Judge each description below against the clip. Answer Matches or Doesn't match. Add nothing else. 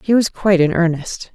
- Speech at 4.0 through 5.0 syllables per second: Doesn't match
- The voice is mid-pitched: Matches